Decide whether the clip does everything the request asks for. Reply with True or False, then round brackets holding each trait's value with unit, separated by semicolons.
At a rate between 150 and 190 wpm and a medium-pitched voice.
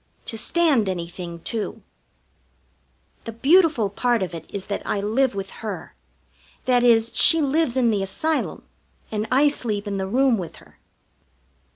False (155 wpm; 225 Hz)